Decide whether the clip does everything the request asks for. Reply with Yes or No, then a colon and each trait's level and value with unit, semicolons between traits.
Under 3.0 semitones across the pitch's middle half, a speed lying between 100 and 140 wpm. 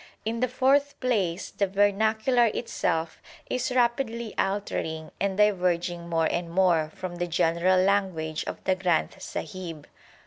No: average, 4.7 semitones; slow, 135 wpm